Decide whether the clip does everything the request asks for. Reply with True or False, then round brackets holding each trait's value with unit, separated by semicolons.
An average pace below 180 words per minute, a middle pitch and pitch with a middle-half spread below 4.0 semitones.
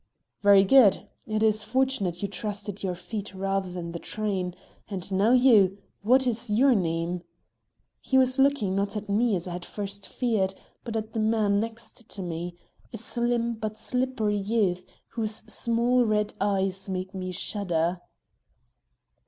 False (160 wpm; 205 Hz; 3.3 semitones)